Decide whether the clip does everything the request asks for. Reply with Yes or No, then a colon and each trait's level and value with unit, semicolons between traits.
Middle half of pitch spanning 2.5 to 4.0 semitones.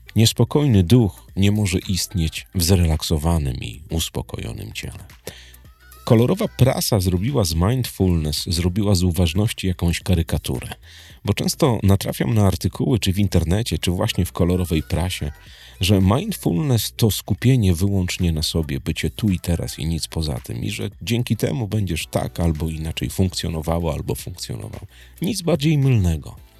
No: average, 5.0 semitones